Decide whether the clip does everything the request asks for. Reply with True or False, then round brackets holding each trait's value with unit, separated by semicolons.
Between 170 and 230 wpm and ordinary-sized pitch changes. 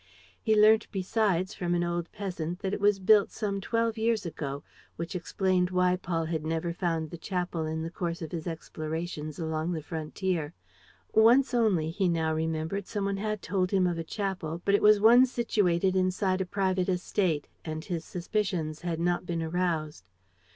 True (180 wpm; 3.4 semitones)